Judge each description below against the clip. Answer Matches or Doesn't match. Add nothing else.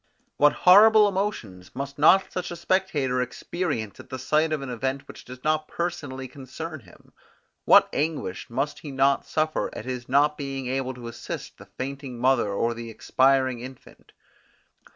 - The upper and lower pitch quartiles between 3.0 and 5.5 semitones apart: Matches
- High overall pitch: Doesn't match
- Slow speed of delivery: Doesn't match